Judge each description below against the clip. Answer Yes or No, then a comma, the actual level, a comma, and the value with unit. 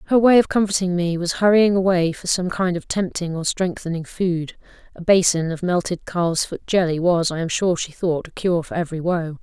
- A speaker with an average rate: No, fast, 210 wpm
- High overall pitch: No, medium, 175 Hz